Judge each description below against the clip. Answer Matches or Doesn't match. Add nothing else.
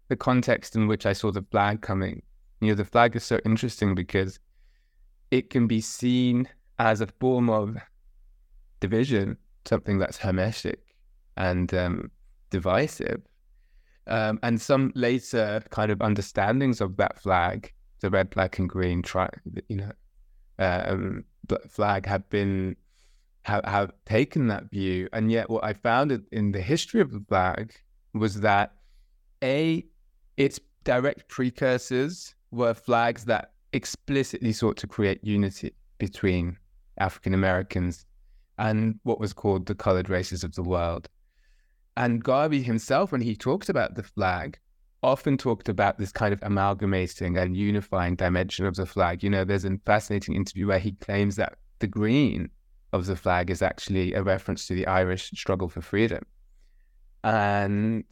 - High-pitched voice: Doesn't match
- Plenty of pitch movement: Doesn't match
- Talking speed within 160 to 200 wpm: Doesn't match